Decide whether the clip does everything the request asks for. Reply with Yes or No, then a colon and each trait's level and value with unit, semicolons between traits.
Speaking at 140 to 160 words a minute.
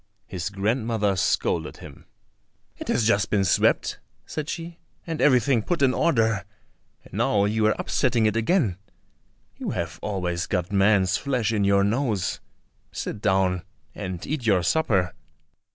Yes: average, 145 wpm